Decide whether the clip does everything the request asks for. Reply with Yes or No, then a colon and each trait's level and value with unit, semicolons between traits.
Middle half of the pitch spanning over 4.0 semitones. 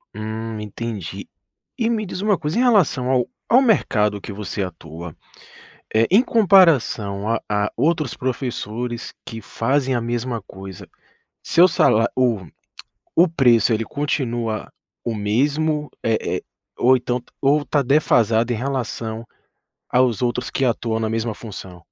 Yes: average, 4.6 semitones